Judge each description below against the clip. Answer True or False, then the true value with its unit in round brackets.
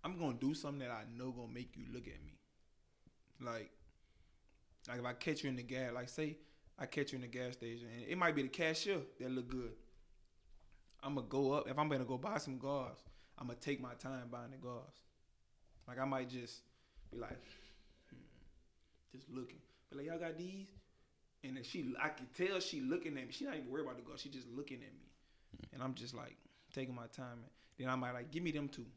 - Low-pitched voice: True (130 Hz)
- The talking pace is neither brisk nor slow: False (225 wpm)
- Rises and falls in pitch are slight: False (3.2 semitones)